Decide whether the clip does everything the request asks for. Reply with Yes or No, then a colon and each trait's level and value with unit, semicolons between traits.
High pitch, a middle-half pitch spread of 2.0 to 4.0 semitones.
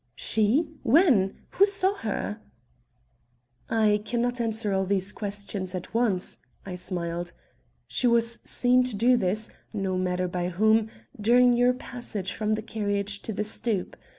Yes: high, 215 Hz; average, 3.7 semitones